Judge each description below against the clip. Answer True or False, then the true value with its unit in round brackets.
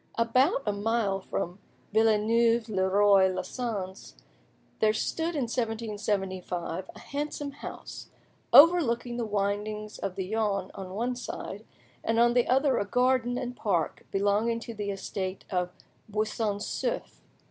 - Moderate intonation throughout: True (3.4 semitones)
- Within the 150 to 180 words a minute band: False (135 wpm)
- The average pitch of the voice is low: False (215 Hz)